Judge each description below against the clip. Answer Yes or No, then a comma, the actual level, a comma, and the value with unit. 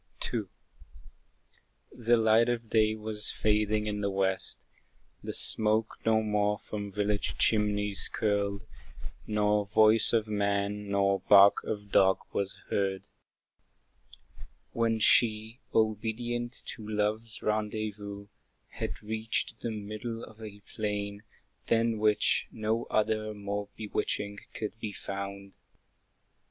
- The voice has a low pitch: Yes, low, 105 Hz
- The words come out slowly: Yes, slow, 115 wpm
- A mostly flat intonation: Yes, narrow, 1.3 semitones